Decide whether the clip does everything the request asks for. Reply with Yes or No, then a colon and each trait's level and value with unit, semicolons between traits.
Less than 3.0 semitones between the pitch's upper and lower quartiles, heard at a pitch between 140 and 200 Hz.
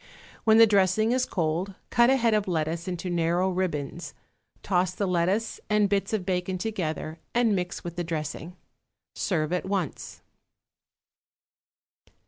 No: average, 3.4 semitones; medium, 185 Hz